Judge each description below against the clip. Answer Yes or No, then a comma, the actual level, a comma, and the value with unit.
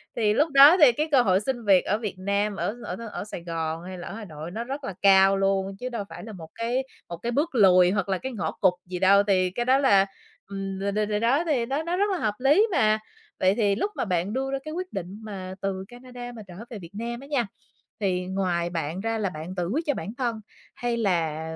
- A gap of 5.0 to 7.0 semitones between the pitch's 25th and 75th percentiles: No, average, 4.6 semitones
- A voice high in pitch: Yes, high, 205 Hz